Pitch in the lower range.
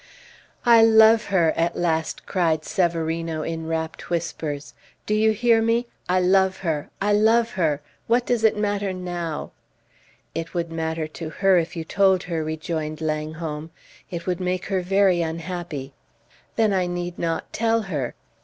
No: medium, 175 Hz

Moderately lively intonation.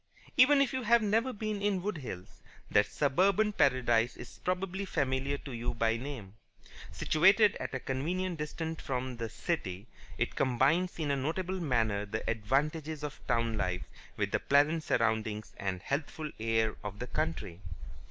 No: wide, 7.9 semitones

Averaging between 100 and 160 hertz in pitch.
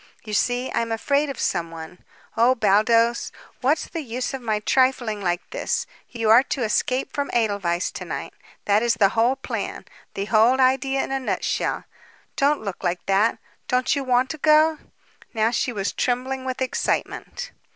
No: high, 240 Hz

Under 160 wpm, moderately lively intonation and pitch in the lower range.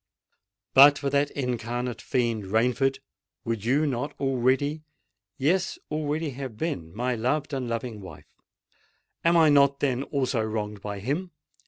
Yes: slow, 135 wpm; average, 3.9 semitones; low, 130 Hz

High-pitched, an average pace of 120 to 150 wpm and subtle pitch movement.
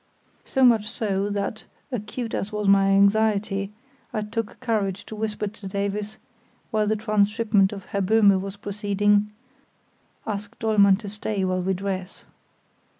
Yes: high, 205 Hz; average, 145 wpm; narrow, 1.6 semitones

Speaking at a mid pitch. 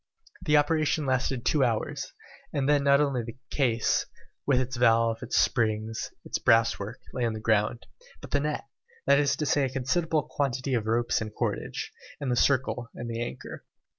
No: low, 125 Hz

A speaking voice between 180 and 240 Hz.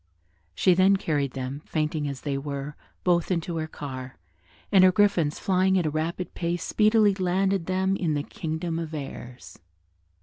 No: medium, 165 Hz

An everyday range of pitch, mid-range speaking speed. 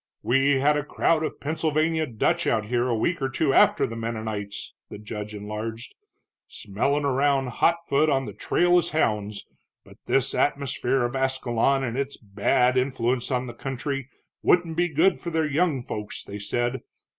Yes: average, 4.2 semitones; average, 170 wpm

